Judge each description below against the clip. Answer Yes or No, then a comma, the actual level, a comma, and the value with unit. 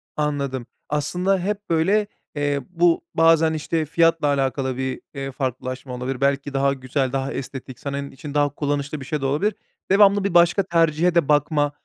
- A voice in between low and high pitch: Yes, medium, 145 Hz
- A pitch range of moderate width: Yes, average, 3.4 semitones